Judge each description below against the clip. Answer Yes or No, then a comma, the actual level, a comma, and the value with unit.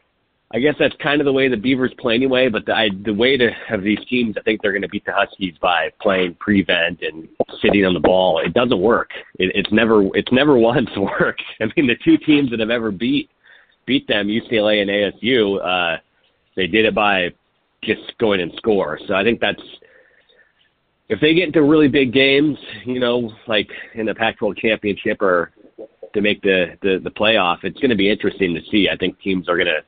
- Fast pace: Yes, fast, 215 wpm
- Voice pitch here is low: Yes, low, 110 Hz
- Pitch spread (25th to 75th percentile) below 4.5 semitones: No, average, 4.8 semitones